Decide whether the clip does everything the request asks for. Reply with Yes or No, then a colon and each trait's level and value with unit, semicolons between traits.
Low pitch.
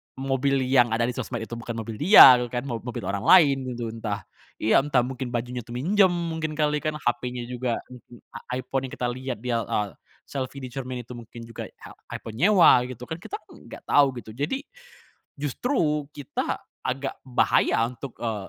Yes: low, 125 Hz